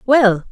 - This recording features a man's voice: No, female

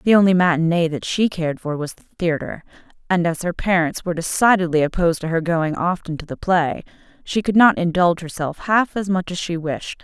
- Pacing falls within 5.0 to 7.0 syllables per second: Yes, 5.7 syllables/s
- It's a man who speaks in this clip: No, female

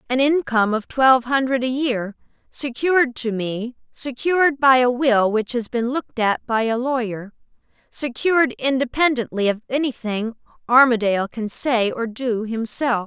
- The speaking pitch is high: Yes, high, 245 Hz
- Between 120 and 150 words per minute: Yes, average, 145 wpm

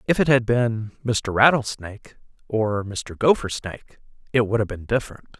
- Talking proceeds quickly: No, average, 155 wpm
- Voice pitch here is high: No, low, 115 Hz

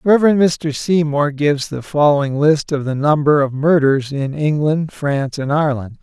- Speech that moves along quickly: No, average, 170 wpm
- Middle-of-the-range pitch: Yes, medium, 145 Hz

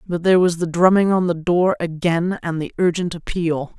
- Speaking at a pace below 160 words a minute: No, fast, 205 wpm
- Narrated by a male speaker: No, female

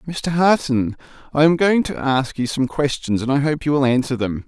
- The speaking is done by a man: Yes, male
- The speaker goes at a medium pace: No, fast, 230 wpm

